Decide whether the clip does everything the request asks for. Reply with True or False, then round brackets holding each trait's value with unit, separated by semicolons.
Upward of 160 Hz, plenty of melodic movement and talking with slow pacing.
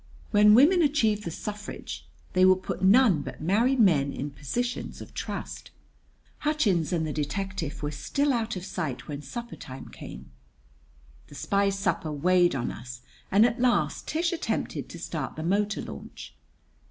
False (190 Hz; 7.2 semitones; 160 wpm)